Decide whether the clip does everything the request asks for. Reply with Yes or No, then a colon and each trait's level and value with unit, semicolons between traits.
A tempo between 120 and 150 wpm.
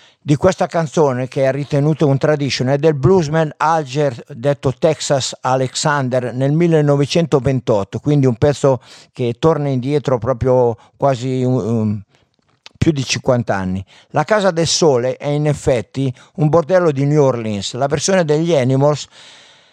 Yes: average, 140 wpm